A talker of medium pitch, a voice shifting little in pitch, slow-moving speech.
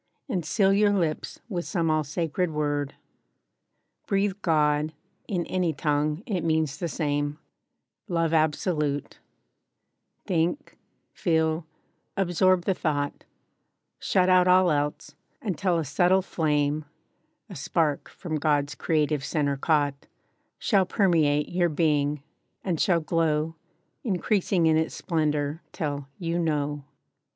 No: medium, 160 Hz; average, 3.2 semitones; slow, 115 wpm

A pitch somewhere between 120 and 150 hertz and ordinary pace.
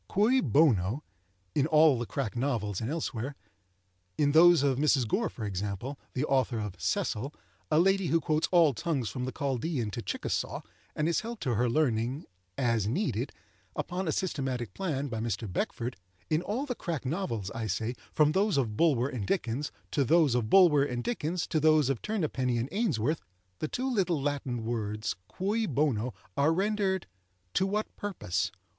Yes: medium, 140 Hz; average, 170 wpm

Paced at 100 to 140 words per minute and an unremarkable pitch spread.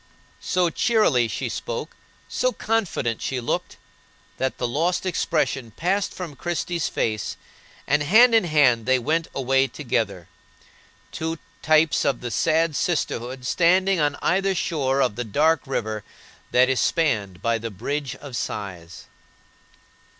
No: slow, 135 wpm; wide, 6.2 semitones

